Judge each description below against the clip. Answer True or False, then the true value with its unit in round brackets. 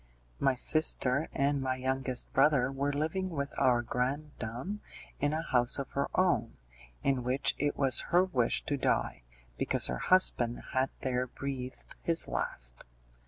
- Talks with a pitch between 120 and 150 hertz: True (135 Hz)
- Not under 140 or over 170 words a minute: True (150 wpm)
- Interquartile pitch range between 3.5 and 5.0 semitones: False (2.6 semitones)